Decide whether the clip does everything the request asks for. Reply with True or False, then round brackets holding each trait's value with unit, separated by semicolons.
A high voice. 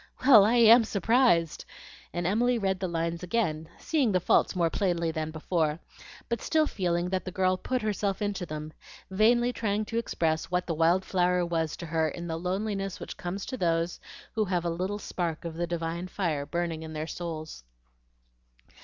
False (180 Hz)